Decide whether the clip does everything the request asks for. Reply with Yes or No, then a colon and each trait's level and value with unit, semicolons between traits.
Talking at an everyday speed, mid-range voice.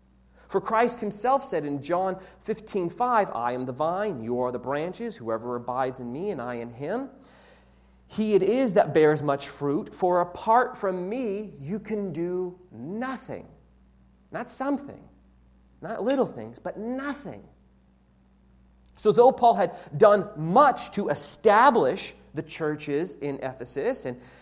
Yes: average, 145 wpm; medium, 170 Hz